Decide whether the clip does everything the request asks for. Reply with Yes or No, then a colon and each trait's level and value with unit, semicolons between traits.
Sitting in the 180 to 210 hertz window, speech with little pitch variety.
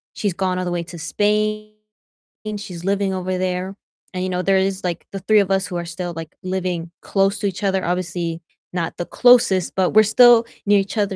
Yes: high, 190 Hz; narrow, 2.1 semitones